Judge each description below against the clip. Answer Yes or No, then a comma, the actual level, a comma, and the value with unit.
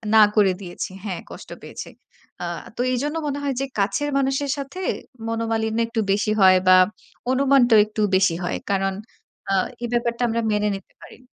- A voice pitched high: Yes, high, 225 Hz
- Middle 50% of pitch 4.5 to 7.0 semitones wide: Yes, average, 5.2 semitones